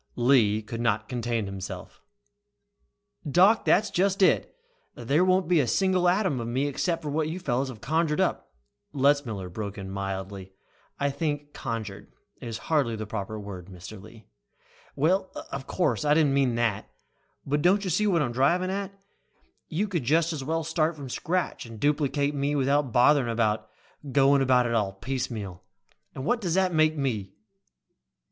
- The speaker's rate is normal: Yes, average, 165 wpm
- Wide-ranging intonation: Yes, wide, 6.5 semitones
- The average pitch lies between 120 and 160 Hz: Yes, low, 135 Hz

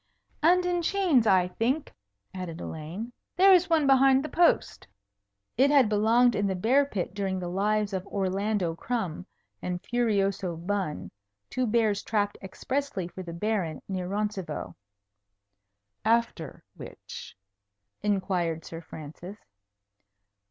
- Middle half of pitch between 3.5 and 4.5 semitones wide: No, average, 5.2 semitones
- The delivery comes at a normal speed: No, slow, 125 wpm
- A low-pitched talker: No, high, 205 Hz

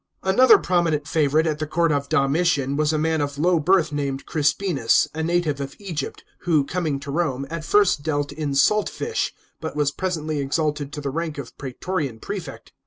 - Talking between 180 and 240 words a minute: Yes, average, 185 wpm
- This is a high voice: No, medium, 155 Hz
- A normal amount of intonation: Yes, average, 3.2 semitones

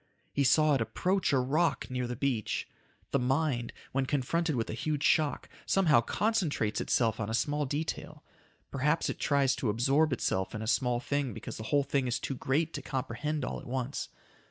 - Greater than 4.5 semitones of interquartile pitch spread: No, average, 3.5 semitones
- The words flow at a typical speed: Yes, average, 190 wpm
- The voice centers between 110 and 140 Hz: Yes, low, 135 Hz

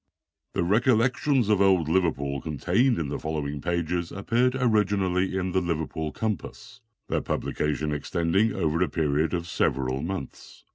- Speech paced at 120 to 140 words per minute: Yes, slow, 135 wpm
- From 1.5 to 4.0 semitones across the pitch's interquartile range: No, average, 4.5 semitones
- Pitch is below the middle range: Yes, very low, 85 Hz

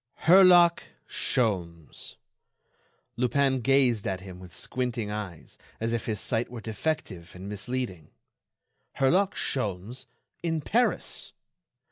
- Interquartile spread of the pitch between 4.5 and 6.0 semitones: Yes, wide, 5.6 semitones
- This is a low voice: Yes, low, 115 Hz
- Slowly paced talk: Yes, slow, 105 wpm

